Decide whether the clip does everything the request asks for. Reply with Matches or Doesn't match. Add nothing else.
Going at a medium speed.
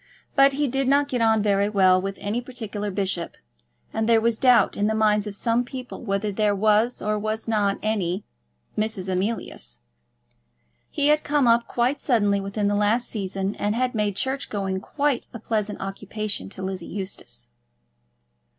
Matches